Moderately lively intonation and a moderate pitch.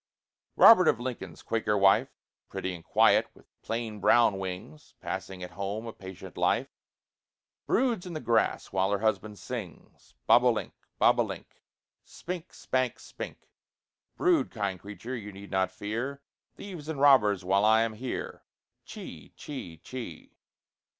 No: average, 5.0 semitones; low, 110 Hz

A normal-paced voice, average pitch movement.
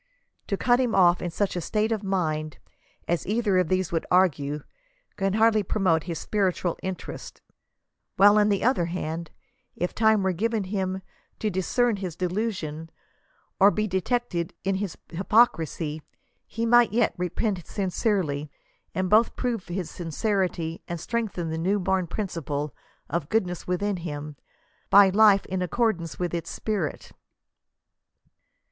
Yes: average, 150 wpm; average, 3.9 semitones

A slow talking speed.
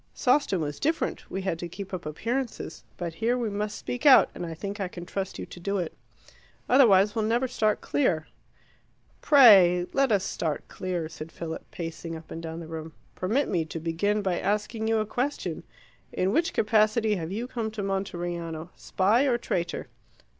No: average, 185 wpm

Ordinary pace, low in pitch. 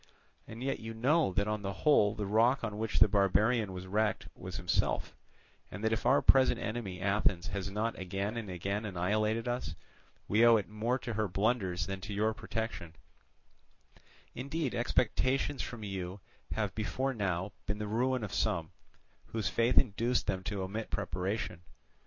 Yes: average, 170 wpm; low, 105 Hz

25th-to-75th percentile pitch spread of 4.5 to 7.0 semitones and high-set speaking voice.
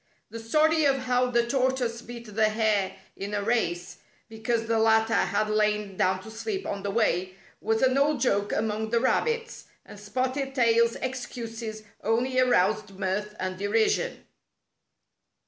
No: average, 3.3 semitones; high, 225 Hz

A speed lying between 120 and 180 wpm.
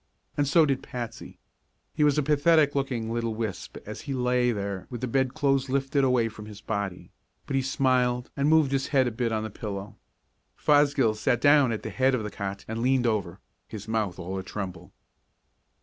No: average, 195 wpm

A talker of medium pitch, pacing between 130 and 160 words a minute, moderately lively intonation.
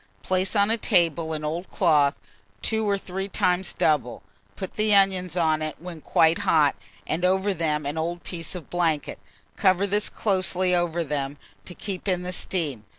No: medium, 175 Hz; average, 175 wpm; average, 3.3 semitones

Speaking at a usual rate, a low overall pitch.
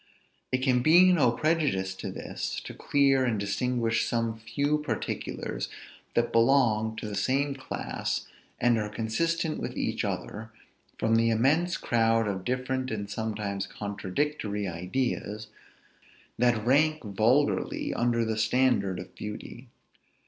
No: slow, 130 wpm; low, 115 Hz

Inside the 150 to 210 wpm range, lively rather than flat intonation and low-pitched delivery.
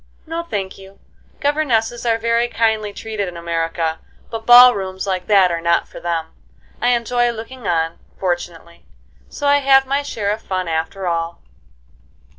No: average, 160 wpm; wide, 5.8 semitones; high, 205 Hz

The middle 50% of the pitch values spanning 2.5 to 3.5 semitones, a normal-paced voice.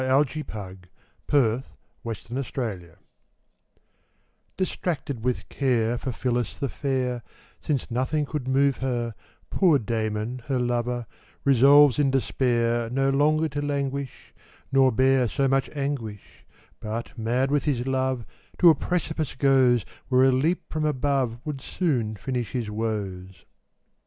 No: average, 3.0 semitones; slow, 130 wpm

